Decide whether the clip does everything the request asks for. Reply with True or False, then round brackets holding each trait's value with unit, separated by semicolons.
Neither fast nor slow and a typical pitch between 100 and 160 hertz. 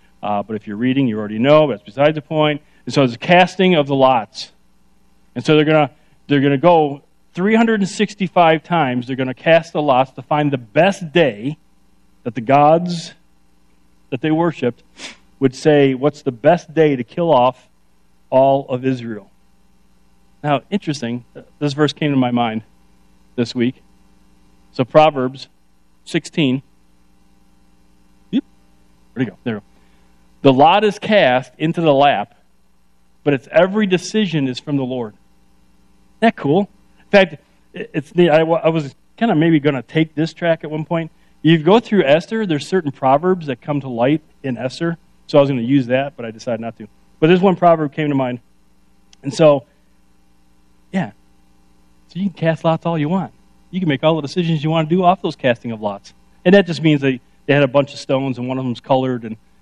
True (185 wpm; 140 Hz)